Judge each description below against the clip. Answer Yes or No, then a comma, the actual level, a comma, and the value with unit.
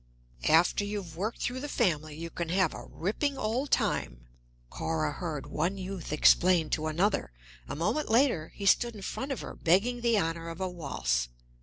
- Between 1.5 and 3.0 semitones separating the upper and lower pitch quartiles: No, wide, 5.4 semitones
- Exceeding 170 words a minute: Yes, average, 180 wpm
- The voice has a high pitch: No, medium, 180 Hz